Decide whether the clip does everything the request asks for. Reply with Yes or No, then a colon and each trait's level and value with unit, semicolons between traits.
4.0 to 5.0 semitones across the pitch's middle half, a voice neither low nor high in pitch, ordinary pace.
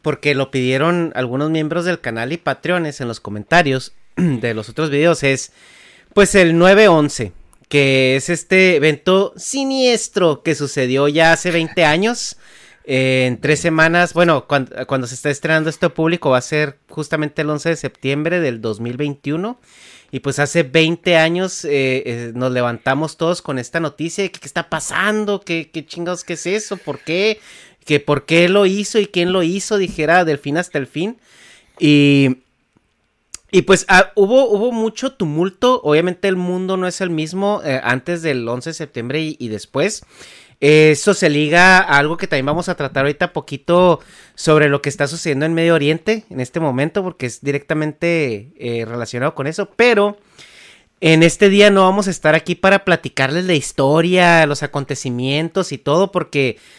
Yes: average, 4.5 semitones; medium, 160 Hz; average, 175 wpm